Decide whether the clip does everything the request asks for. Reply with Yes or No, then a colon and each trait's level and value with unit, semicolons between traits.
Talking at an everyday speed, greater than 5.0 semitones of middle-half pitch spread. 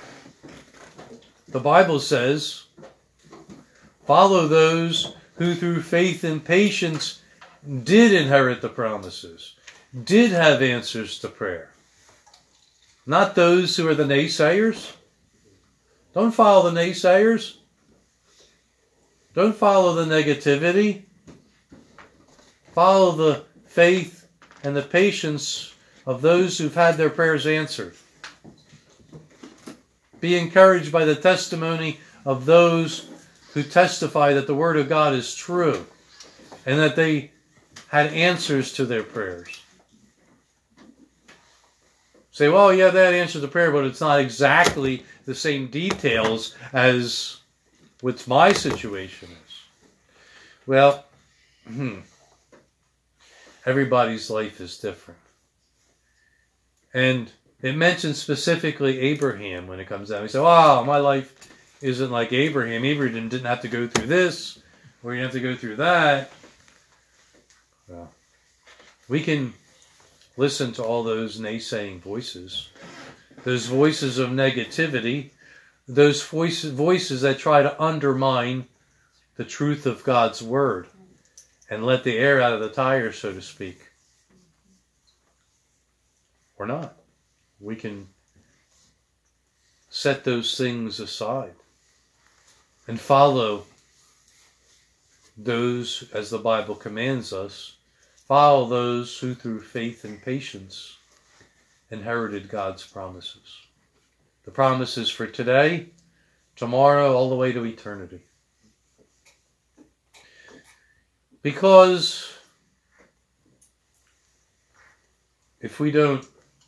No: slow, 105 wpm; wide, 5.5 semitones